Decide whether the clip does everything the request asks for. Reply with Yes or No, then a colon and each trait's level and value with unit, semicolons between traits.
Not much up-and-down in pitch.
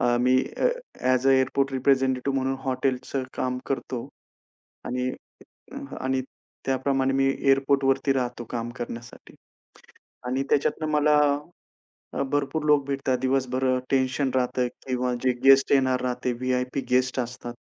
Yes: narrow, 1.2 semitones